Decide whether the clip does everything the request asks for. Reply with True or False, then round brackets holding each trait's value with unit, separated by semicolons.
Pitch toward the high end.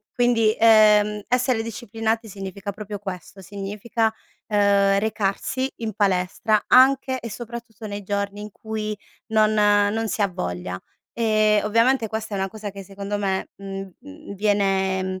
True (210 Hz)